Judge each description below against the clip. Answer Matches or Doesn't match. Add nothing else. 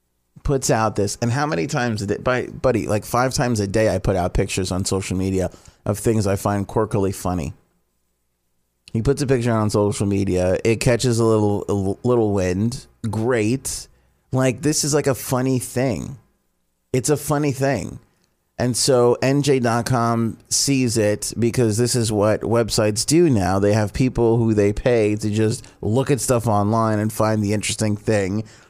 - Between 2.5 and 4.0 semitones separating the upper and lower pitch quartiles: Matches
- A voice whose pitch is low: Matches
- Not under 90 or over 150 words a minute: Doesn't match